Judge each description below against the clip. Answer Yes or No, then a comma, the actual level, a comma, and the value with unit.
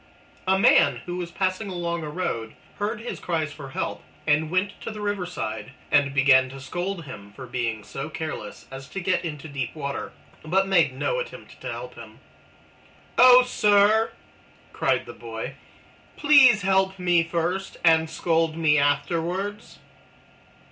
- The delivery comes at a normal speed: Yes, average, 155 wpm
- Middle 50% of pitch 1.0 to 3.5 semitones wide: No, wide, 5.4 semitones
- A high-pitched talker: No, medium, 170 Hz